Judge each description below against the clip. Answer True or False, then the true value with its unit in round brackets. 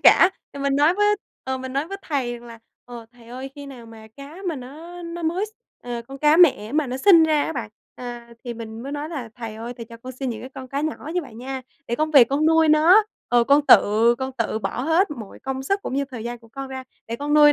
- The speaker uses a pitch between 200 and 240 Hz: False (270 Hz)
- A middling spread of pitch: True (4.4 semitones)